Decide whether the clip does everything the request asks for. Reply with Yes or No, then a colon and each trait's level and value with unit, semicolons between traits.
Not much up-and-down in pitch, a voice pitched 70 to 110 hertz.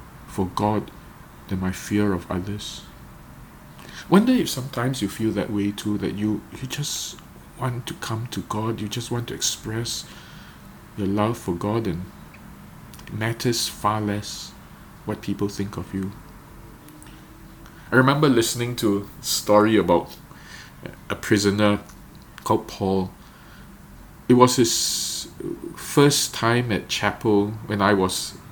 No: average, 3.2 semitones; low, 105 Hz